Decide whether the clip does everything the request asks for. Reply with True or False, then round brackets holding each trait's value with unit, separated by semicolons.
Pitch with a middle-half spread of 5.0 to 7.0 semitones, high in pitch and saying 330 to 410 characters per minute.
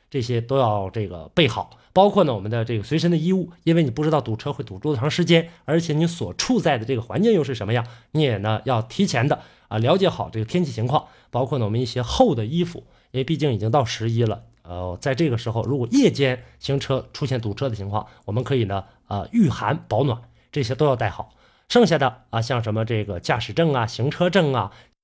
False (5.3 semitones; 130 Hz; 340 characters per minute)